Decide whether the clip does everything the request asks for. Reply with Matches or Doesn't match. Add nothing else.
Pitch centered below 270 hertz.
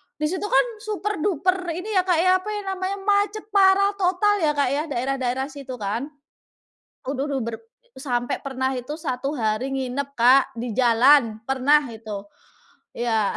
Doesn't match